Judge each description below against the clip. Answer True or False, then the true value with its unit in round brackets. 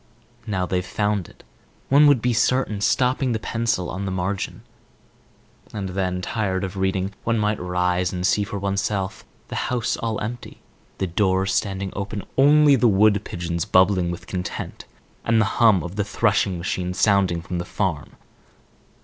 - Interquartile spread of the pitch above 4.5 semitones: False (3.0 semitones)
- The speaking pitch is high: False (100 Hz)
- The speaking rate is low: False (165 wpm)